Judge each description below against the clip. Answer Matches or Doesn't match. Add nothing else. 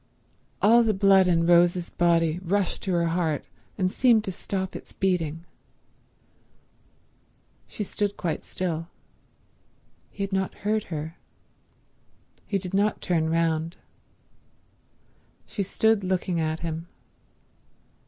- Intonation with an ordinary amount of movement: Matches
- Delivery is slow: Matches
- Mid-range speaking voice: Matches